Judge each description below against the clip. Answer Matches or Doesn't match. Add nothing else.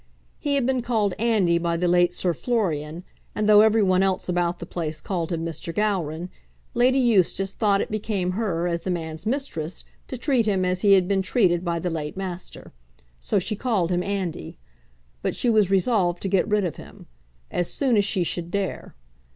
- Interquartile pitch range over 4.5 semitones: Doesn't match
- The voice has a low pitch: Doesn't match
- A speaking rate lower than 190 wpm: Doesn't match